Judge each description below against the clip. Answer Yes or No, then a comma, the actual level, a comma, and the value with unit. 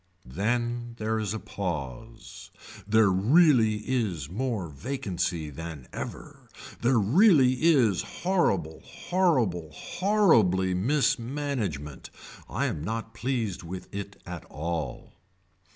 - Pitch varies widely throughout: Yes, wide, 6.4 semitones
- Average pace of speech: No, slow, 105 wpm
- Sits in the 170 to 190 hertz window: No, low, 110 Hz